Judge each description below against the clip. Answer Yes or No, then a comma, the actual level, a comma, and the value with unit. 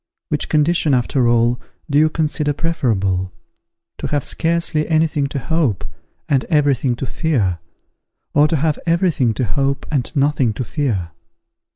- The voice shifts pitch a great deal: No, average, 4.6 semitones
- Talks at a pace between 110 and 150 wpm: No, average, 160 wpm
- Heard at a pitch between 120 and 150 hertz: Yes, medium, 140 Hz